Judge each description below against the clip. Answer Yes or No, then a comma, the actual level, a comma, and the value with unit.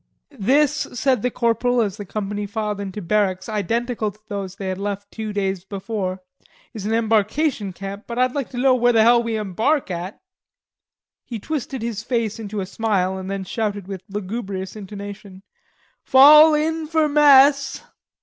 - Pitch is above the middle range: Yes, high, 215 Hz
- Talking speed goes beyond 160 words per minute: Yes, average, 170 wpm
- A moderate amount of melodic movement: Yes, average, 3.9 semitones